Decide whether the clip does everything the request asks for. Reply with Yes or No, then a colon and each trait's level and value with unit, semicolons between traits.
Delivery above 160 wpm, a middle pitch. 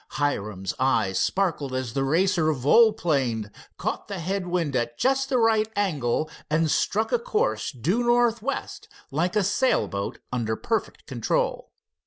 No: average, 145 wpm; medium, 170 Hz